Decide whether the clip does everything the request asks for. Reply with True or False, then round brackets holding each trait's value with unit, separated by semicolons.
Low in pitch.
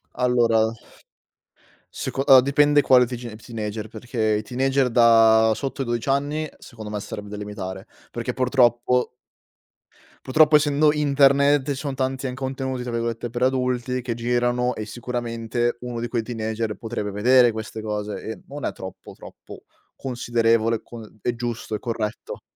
True (120 Hz)